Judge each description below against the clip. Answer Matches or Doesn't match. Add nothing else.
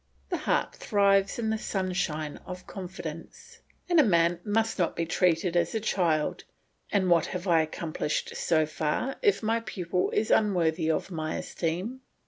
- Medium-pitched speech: Matches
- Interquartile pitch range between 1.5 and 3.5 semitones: Doesn't match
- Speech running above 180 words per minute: Doesn't match